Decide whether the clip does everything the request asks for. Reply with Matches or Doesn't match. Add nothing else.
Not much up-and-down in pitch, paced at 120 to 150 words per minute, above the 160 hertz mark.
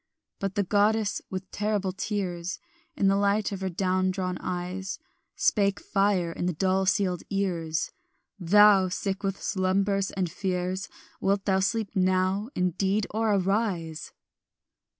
Matches